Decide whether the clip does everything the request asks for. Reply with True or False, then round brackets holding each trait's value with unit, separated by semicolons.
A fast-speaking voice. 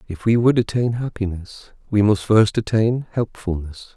False (150 wpm)